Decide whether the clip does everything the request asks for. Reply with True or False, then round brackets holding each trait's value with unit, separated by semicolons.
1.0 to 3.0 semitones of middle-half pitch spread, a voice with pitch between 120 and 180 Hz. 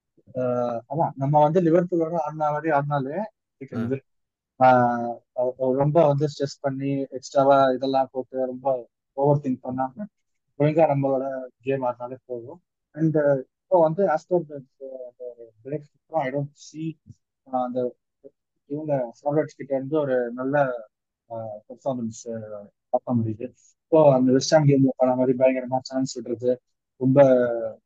True (2.7 semitones; 135 Hz)